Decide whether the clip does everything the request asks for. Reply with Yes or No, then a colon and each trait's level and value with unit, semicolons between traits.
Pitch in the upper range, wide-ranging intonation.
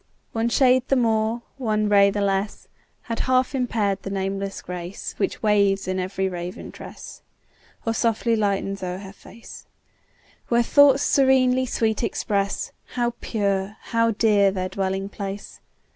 No: high, 210 Hz; average, 3.1 semitones